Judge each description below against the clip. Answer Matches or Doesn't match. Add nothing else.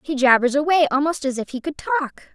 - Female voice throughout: Matches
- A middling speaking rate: Doesn't match